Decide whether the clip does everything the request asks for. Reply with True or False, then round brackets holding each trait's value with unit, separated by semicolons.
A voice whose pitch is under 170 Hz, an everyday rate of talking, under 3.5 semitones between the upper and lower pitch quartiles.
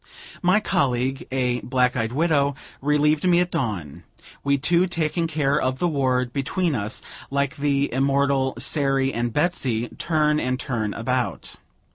True (135 Hz; 145 wpm; 3.1 semitones)